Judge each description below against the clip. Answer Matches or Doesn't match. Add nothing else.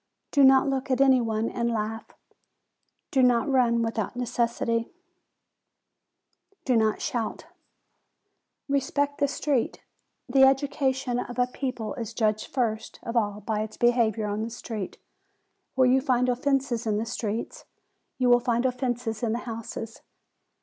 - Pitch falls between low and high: Doesn't match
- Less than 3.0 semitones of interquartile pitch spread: Matches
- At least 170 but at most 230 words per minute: Doesn't match